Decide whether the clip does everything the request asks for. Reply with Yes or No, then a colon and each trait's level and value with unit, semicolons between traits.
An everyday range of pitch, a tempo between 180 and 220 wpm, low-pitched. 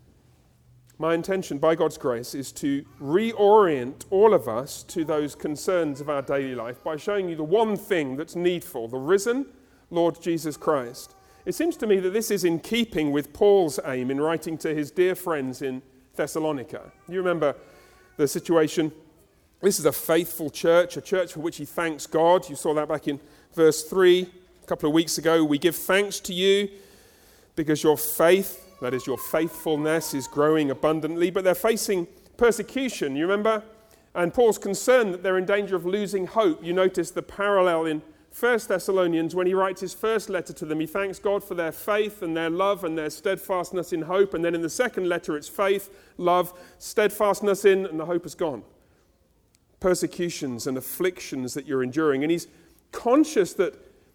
No: average, 4.1 semitones; average, 185 wpm; medium, 175 Hz